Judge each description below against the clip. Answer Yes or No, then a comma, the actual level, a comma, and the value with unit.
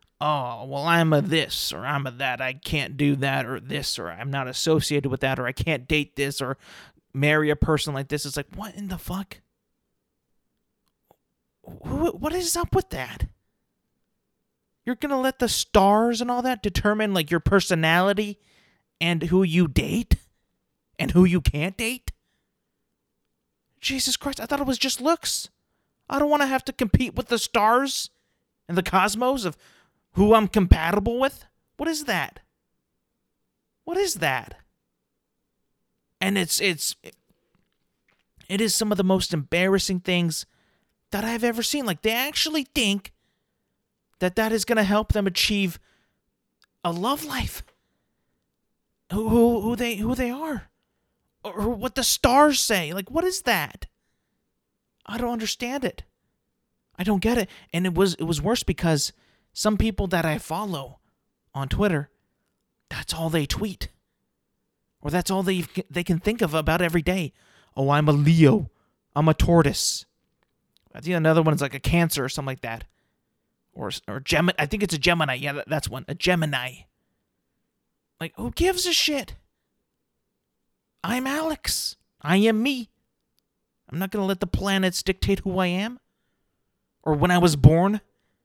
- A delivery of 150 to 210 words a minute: Yes, average, 160 wpm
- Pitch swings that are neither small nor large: No, wide, 7.0 semitones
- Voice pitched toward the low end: No, high, 190 Hz